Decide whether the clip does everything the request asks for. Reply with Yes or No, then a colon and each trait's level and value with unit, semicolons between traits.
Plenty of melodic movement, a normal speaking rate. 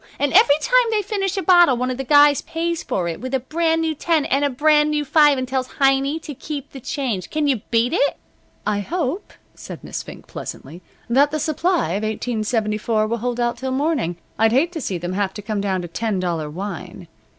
No: wide, 6.3 semitones; fast, 220 wpm